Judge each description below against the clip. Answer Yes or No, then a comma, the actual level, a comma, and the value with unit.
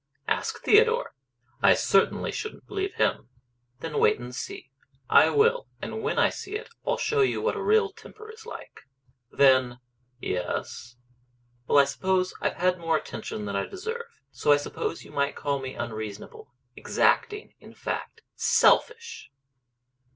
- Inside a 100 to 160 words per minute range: Yes, average, 155 wpm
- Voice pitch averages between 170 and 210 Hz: Yes, high, 190 Hz